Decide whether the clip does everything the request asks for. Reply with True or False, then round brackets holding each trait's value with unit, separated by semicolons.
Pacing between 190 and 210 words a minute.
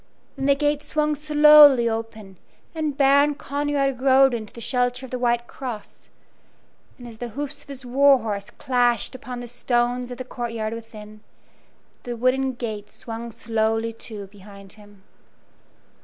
False (155 wpm)